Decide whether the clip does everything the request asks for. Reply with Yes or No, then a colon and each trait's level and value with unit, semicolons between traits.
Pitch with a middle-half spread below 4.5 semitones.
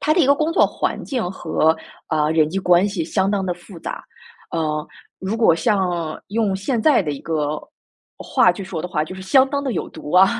No: average, 5.0 semitones